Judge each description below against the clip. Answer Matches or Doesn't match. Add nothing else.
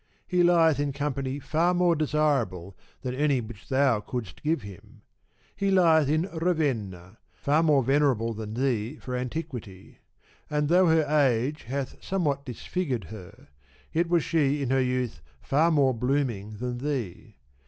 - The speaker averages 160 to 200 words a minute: Doesn't match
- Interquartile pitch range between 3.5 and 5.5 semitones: Matches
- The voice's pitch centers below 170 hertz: Matches